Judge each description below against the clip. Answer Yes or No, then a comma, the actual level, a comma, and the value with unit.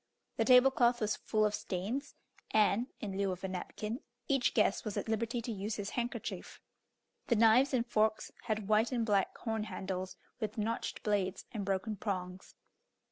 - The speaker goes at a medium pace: Yes, average, 175 wpm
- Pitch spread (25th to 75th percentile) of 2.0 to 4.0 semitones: Yes, average, 2.8 semitones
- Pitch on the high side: Yes, high, 215 Hz